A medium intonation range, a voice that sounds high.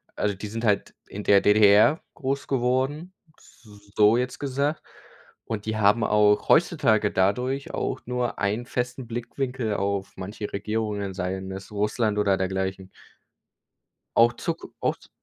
No: average, 3.7 semitones; low, 110 Hz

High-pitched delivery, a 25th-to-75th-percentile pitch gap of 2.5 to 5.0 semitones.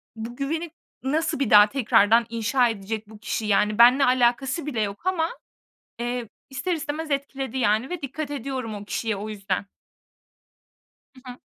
Yes: high, 245 Hz; average, 4.3 semitones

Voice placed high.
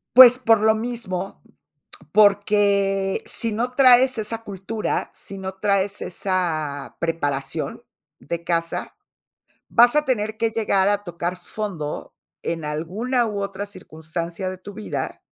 Yes: high, 200 Hz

